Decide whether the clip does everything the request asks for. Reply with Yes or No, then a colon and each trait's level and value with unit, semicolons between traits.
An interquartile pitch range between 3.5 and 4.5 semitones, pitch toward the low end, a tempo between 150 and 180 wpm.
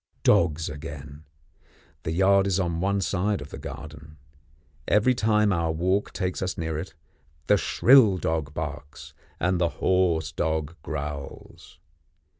No: average, 3.9 semitones; very low, 85 Hz; slow, 135 wpm